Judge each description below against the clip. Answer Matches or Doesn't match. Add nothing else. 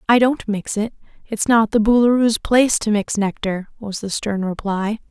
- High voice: Matches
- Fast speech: Doesn't match